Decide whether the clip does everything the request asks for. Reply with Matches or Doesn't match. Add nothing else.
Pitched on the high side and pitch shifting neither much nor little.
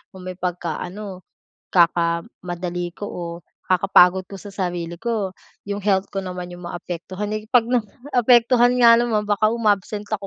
Matches